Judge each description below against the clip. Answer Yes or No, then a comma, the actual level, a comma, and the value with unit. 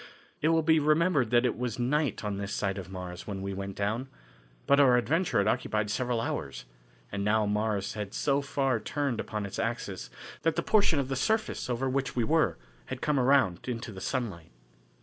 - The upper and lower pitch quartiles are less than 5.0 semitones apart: No, wide, 5.6 semitones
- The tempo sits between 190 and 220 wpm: Yes, average, 200 wpm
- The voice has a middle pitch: No, low, 120 Hz